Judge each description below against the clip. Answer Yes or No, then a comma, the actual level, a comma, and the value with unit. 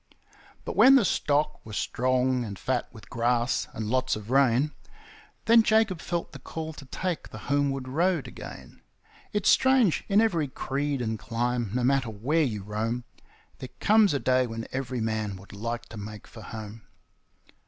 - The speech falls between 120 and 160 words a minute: No, average, 170 wpm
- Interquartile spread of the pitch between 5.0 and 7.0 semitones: Yes, average, 5.3 semitones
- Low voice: Yes, low, 130 Hz